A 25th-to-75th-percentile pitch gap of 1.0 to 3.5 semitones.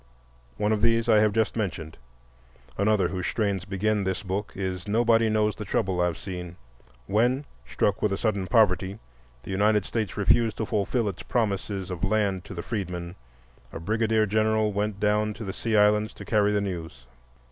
Yes: narrow, 2.4 semitones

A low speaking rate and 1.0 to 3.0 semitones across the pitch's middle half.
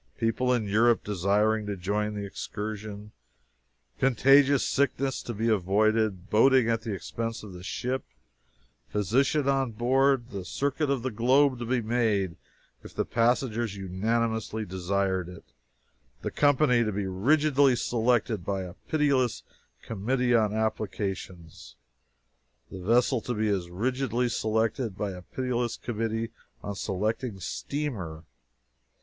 No: slow, 130 wpm; average, 3.8 semitones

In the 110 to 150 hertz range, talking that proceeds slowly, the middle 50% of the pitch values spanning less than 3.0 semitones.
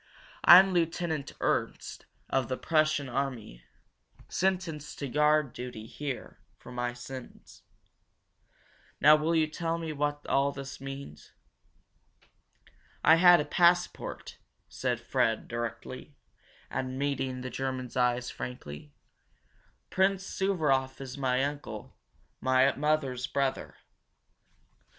No: medium, 140 Hz; slow, 110 wpm; average, 3.3 semitones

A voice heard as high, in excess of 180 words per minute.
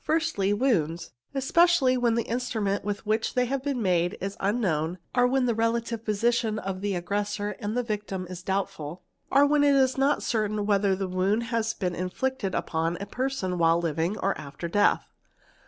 Yes: high, 210 Hz; average, 190 wpm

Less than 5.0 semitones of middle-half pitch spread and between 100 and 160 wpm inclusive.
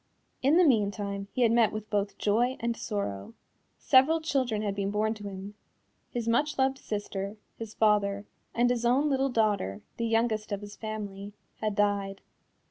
No: average, 3.0 semitones; average, 170 wpm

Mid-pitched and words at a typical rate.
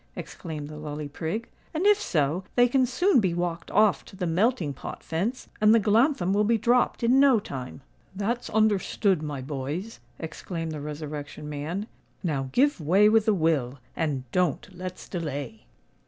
Yes: medium, 180 Hz; average, 170 wpm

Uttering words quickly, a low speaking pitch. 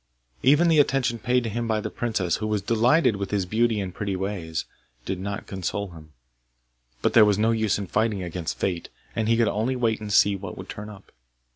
Yes: fast, 215 wpm; low, 105 Hz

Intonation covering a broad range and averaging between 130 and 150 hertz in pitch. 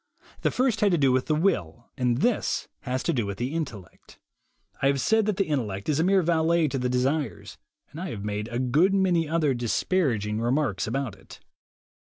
Yes: wide, 5.9 semitones; medium, 140 Hz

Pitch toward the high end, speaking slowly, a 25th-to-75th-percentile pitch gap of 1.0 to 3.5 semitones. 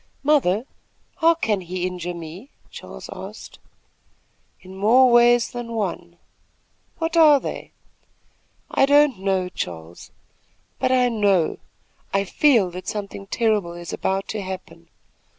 No: high, 200 Hz; slow, 125 wpm; average, 5.3 semitones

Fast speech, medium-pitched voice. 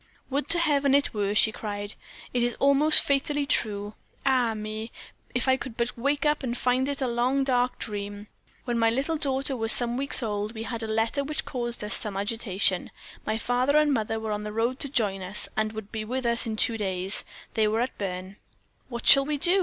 No: fast, 225 wpm; high, 235 Hz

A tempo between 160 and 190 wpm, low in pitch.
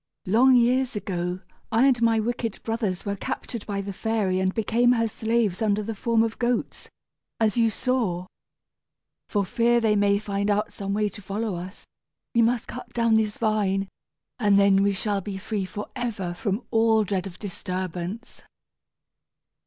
No: average, 170 wpm; high, 210 Hz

